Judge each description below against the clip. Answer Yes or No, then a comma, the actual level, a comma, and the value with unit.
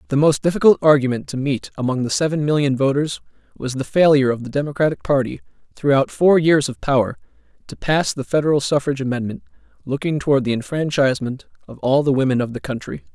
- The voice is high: No, medium, 140 Hz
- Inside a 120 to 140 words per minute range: No, average, 185 wpm